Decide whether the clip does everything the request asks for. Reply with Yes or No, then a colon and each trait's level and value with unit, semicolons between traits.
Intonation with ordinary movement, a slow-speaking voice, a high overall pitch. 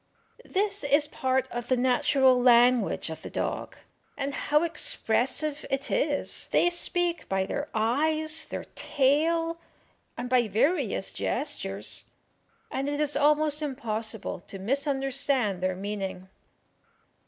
Yes: average, 4.3 semitones; slow, 120 wpm; very high, 270 Hz